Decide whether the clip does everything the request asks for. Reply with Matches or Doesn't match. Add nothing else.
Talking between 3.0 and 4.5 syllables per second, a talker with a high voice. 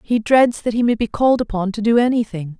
Doesn't match